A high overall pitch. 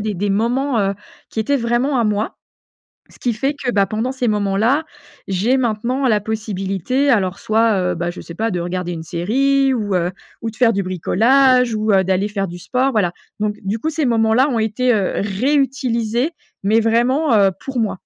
Yes: high, 220 Hz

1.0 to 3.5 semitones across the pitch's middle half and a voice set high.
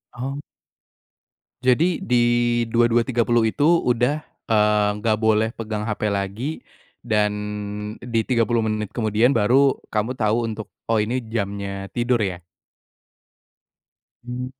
No: narrow, 2.5 semitones; low, 115 Hz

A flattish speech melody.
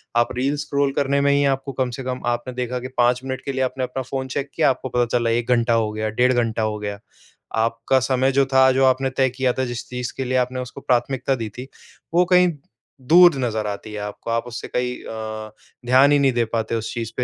Yes: narrow, 2.3 semitones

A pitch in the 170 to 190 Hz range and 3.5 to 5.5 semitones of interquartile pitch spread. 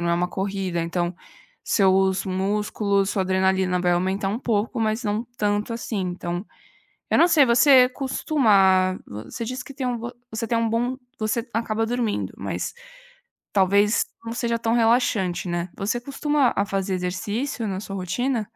No: high, 210 Hz; average, 3.8 semitones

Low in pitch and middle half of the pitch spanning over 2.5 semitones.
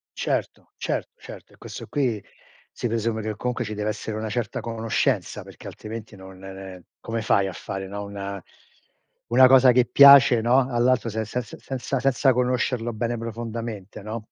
Yes: low, 115 Hz; average, 2.9 semitones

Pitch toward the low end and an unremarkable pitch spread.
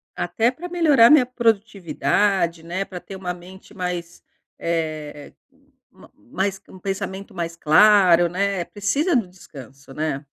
No: high, 190 Hz; average, 3.6 semitones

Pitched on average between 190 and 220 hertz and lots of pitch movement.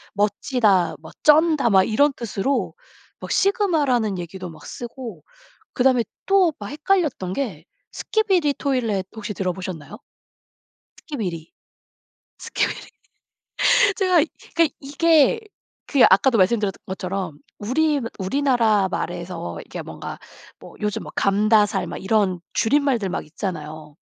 Yes: high, 215 Hz; wide, 7.2 semitones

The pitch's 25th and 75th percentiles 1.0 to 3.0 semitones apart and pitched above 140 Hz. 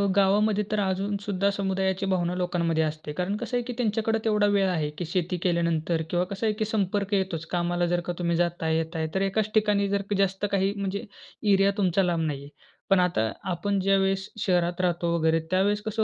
Yes: narrow, 2.6 semitones; high, 190 Hz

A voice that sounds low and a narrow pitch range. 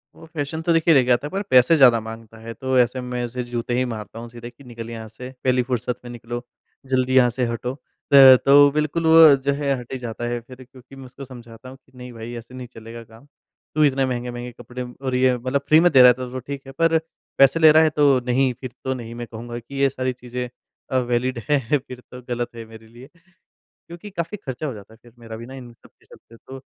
Yes: low, 125 Hz; narrow, 2.3 semitones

